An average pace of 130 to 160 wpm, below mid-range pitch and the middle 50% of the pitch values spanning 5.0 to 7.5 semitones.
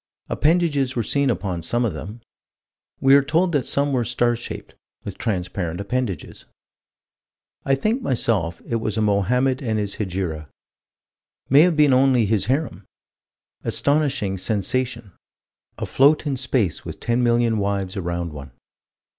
Yes: average, 140 wpm; low, 120 Hz; wide, 5.5 semitones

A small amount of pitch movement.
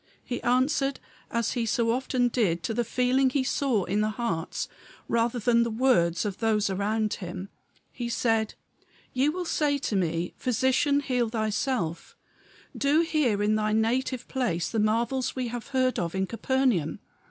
No: average, 3.5 semitones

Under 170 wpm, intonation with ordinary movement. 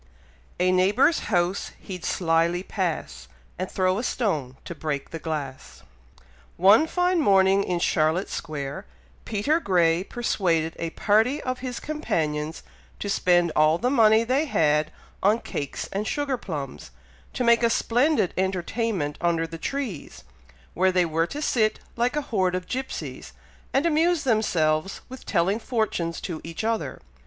No: average, 145 wpm; wide, 6.3 semitones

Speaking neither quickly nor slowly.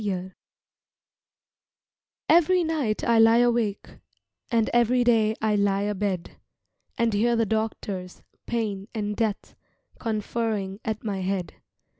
No: slow, 115 wpm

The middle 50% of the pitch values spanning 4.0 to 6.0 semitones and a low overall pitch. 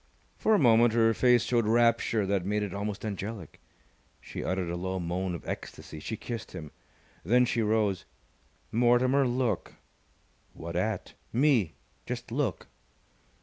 Yes: average, 4.3 semitones; low, 110 Hz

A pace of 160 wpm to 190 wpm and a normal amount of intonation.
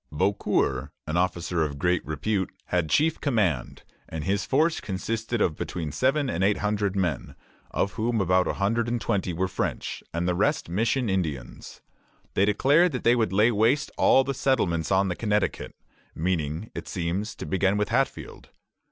Yes: average, 170 wpm; average, 4.7 semitones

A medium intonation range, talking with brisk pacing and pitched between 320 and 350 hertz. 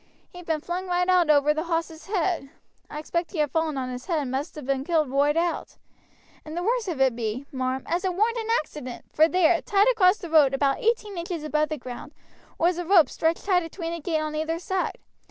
Yes: average, 3.5 semitones; fast, 230 wpm; very high, 325 Hz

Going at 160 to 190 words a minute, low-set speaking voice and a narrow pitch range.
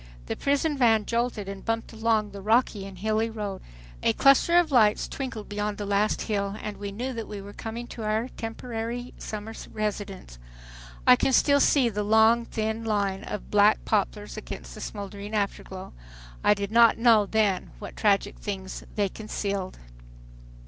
No: average, 170 wpm; high, 215 Hz; narrow, 2.2 semitones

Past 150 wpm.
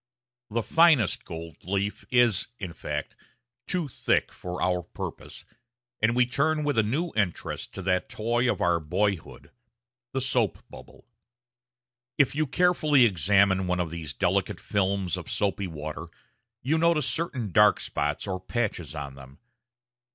No: average, 145 wpm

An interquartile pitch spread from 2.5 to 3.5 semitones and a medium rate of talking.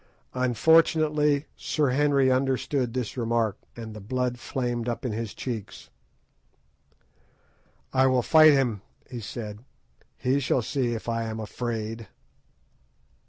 No: average, 3.0 semitones; slow, 120 wpm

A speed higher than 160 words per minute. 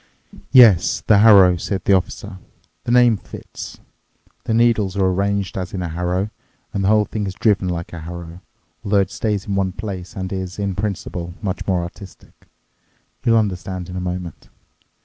Yes: average, 175 wpm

